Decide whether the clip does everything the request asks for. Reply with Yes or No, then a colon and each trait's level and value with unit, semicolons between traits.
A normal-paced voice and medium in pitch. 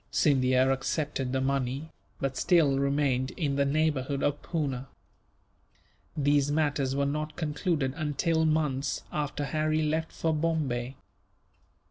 No: slow, 120 wpm; medium, 145 Hz